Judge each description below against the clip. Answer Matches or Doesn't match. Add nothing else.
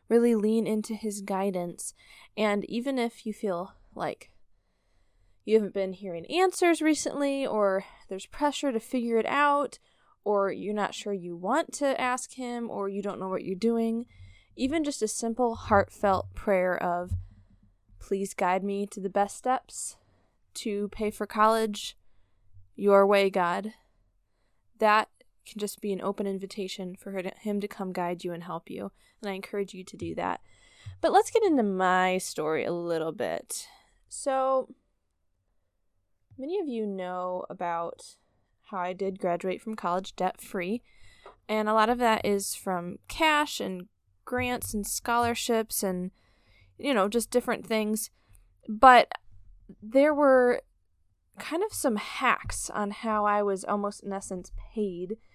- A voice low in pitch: Doesn't match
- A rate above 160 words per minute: Doesn't match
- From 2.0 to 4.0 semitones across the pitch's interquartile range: Doesn't match